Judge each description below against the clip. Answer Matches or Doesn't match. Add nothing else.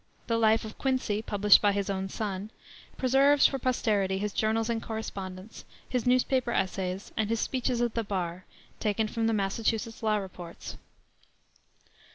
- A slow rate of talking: Doesn't match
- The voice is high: Matches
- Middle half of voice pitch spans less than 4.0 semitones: Matches